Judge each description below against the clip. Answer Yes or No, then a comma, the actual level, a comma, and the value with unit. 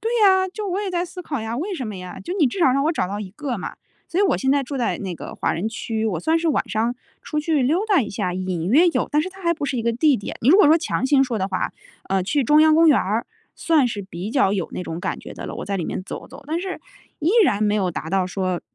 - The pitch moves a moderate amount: No, wide, 8.4 semitones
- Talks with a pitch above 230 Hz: Yes, very high, 265 Hz